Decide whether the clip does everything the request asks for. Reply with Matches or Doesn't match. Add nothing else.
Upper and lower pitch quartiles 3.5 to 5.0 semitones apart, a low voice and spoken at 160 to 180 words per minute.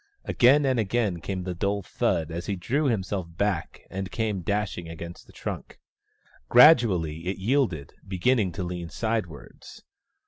Doesn't match